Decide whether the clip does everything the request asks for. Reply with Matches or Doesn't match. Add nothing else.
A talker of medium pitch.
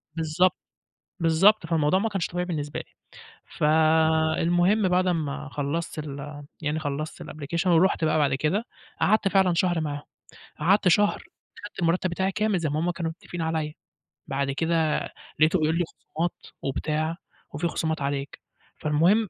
Matches